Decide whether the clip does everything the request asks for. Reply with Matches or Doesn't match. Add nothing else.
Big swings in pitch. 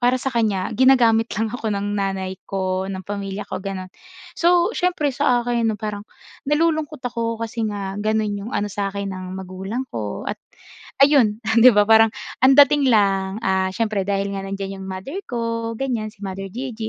Doesn't match